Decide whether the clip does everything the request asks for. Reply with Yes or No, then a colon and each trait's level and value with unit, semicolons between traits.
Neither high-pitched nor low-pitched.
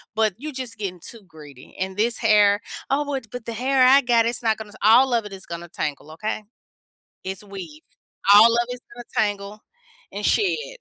No: high, 220 Hz